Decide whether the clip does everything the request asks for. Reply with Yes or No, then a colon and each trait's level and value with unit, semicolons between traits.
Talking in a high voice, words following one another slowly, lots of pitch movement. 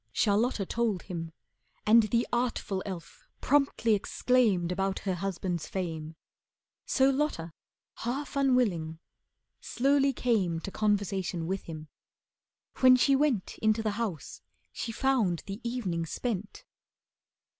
Yes: high, 210 Hz; slow, 115 wpm; wide, 5.7 semitones